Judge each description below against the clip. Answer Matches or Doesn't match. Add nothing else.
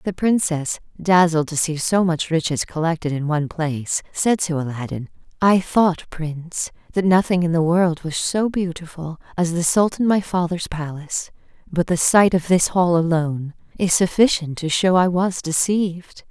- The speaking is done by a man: Doesn't match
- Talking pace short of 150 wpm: Doesn't match